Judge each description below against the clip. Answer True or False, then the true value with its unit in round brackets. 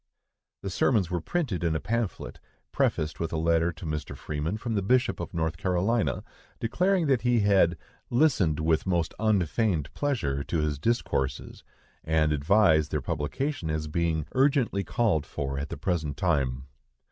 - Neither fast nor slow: True (160 wpm)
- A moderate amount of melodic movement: False (6.5 semitones)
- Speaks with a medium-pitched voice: False (85 Hz)